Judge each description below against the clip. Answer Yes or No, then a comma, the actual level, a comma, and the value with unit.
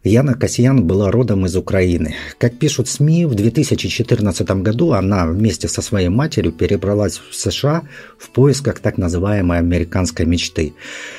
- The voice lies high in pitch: No, low, 105 Hz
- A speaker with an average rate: Yes, average, 140 wpm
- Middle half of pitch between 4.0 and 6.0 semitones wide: Yes, average, 5.2 semitones